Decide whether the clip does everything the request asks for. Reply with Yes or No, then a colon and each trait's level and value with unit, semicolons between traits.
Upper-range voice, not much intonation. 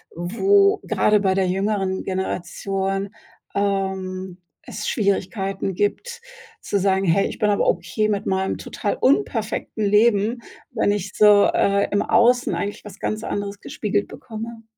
Yes: high, 200 Hz; narrow, 2.0 semitones